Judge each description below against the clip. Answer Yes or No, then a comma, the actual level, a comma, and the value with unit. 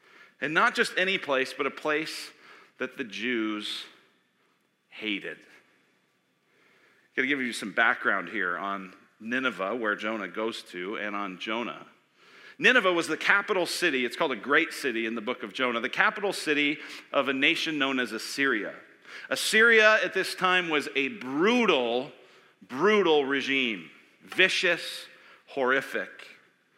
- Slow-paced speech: No, average, 145 wpm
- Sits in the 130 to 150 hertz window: Yes, low, 135 Hz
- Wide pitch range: Yes, wide, 7.9 semitones